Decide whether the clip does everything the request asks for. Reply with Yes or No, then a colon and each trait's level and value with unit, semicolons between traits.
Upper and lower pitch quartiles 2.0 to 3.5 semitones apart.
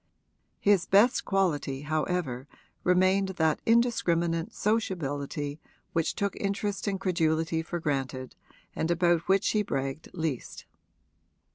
No: average, 4.6 semitones